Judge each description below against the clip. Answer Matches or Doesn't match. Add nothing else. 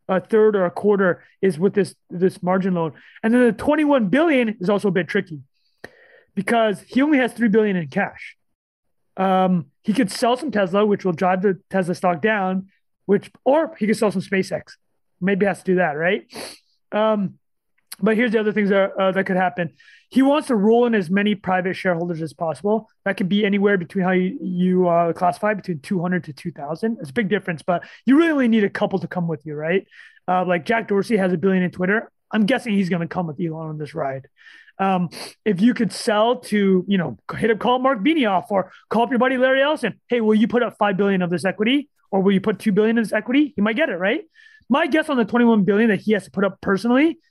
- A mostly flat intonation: Doesn't match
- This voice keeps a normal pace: Doesn't match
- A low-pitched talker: Doesn't match